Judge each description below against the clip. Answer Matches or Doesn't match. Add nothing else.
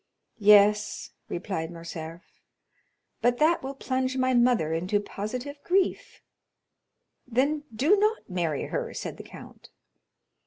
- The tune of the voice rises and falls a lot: Matches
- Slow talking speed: Matches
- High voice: Matches